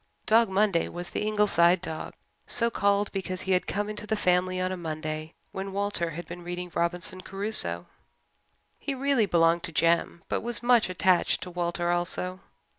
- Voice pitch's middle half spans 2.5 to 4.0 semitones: Yes, average, 3.1 semitones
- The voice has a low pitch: No, medium, 185 Hz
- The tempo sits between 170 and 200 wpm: Yes, average, 175 wpm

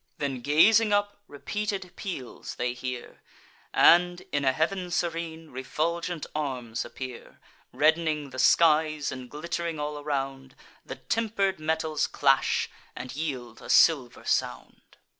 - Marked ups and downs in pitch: No, average, 4.2 semitones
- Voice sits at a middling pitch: Yes, medium, 155 Hz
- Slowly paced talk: Yes, slow, 120 wpm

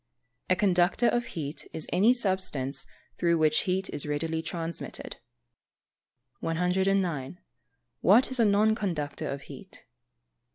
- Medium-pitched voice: Yes, medium, 180 Hz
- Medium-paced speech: No, slow, 125 wpm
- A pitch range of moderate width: Yes, average, 3.9 semitones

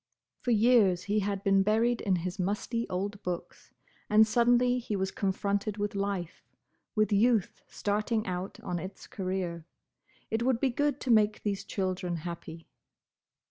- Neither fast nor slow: Yes, average, 150 wpm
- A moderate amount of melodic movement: Yes, average, 3.1 semitones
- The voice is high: Yes, high, 205 Hz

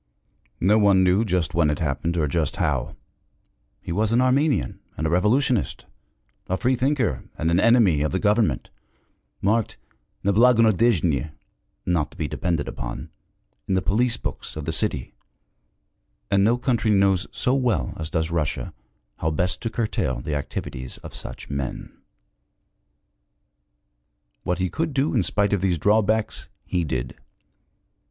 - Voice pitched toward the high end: No, very low, 95 Hz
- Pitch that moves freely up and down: Yes, wide, 6.0 semitones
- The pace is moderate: Yes, average, 145 wpm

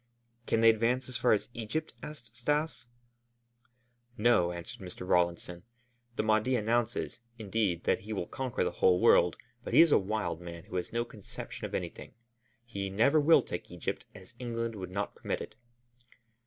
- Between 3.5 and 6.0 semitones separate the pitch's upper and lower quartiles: Yes, average, 4.7 semitones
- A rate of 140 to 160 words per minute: No, average, 170 wpm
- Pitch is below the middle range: Yes, low, 110 Hz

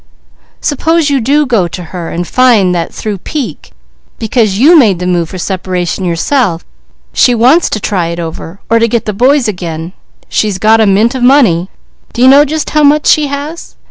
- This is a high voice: Yes, high, 220 Hz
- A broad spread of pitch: Yes, wide, 7.3 semitones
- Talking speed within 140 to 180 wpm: No, average, 195 wpm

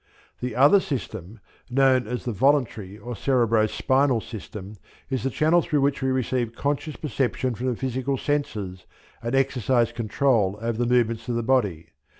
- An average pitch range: Yes, average, 3.1 semitones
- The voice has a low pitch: Yes, low, 125 Hz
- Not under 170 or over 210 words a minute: No, average, 160 wpm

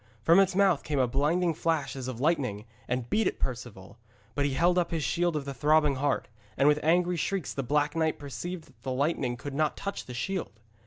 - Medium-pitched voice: Yes, medium, 150 Hz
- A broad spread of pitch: No, average, 4.4 semitones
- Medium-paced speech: No, fast, 220 wpm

